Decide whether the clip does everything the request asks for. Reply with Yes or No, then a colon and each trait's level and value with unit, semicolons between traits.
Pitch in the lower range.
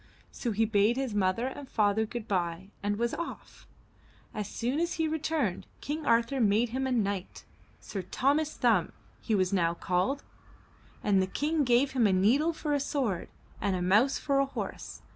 No: high, 230 Hz